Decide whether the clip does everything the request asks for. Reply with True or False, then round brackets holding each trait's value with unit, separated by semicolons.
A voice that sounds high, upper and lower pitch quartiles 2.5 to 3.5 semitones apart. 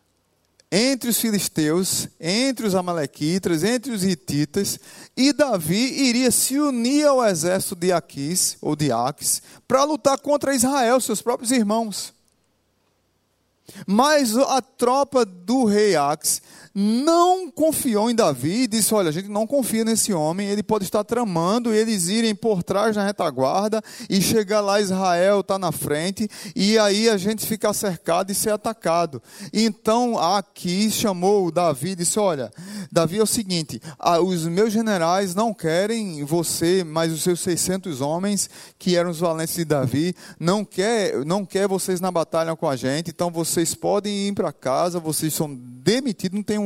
False (200 Hz; 4.8 semitones)